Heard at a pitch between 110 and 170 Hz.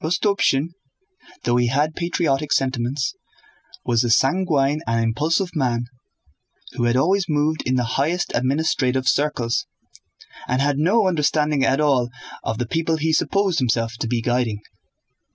Yes: medium, 140 Hz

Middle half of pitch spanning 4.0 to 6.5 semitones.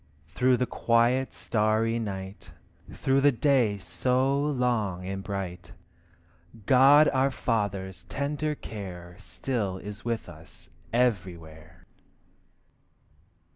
Yes: average, 5.3 semitones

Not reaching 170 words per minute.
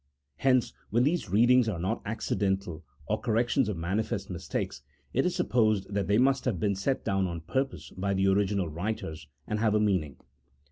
No: average, 185 wpm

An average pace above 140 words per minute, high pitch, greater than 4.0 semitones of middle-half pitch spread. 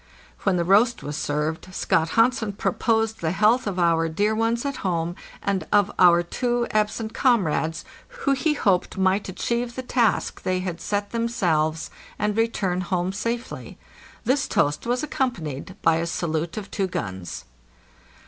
Yes: average, 155 wpm; high, 200 Hz; wide, 5.4 semitones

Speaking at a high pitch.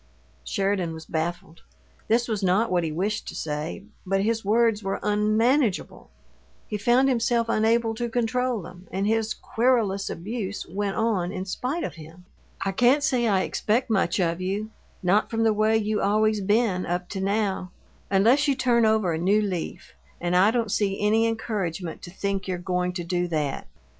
Yes: high, 205 Hz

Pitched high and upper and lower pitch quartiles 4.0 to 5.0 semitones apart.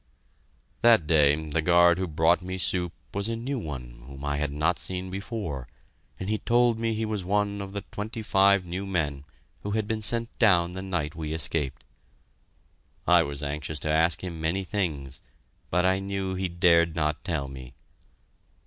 No: very low, 90 Hz; average, 4.6 semitones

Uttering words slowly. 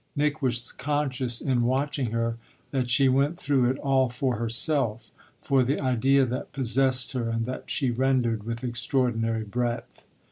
No: average, 155 wpm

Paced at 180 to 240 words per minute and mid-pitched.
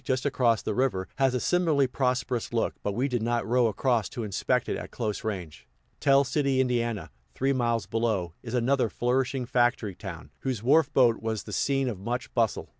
No: average, 190 wpm; low, 120 Hz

